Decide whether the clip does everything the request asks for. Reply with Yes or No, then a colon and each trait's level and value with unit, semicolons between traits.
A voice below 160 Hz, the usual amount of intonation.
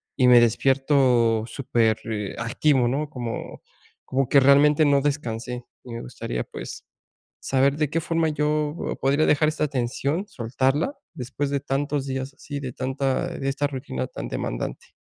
Yes: low, 135 Hz; average, 3.1 semitones